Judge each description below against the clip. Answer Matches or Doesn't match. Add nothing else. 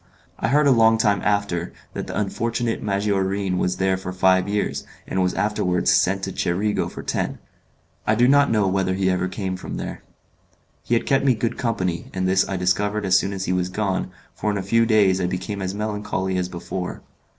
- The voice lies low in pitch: Matches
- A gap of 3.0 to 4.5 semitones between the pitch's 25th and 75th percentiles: Doesn't match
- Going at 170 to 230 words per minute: Matches